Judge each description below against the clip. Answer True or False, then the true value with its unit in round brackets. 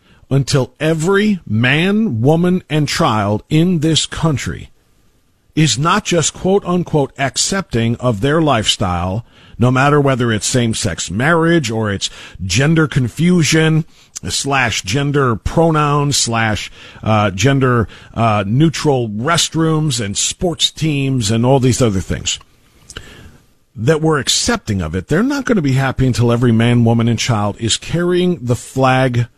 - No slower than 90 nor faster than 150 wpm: True (135 wpm)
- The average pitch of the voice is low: True (130 Hz)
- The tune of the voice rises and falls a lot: True (5.7 semitones)